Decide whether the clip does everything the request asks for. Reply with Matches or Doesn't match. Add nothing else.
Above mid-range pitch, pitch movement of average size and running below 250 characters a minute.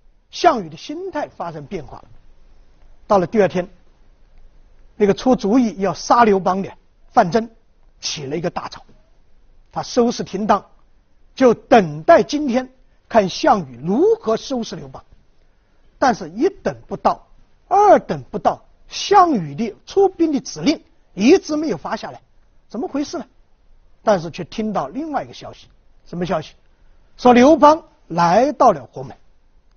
Doesn't match